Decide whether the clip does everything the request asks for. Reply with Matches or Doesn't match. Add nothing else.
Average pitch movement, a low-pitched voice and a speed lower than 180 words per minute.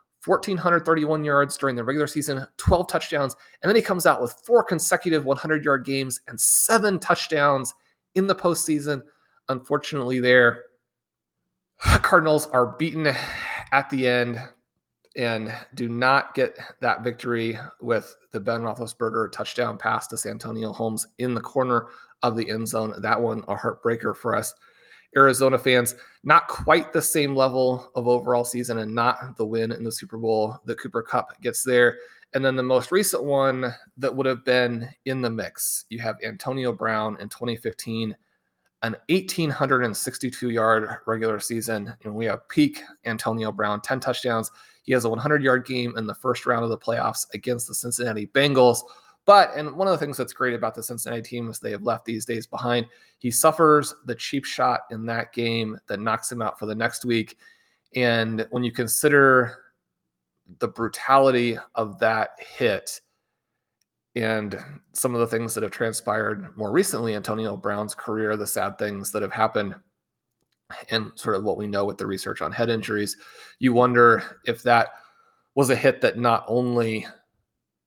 Matches